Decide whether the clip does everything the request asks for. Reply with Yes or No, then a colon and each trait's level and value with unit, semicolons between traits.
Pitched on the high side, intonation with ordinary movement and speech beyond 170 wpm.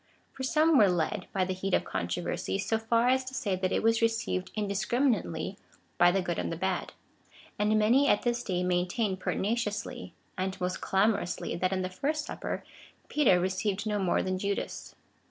Yes: high, 200 Hz; average, 3.7 semitones; average, 185 wpm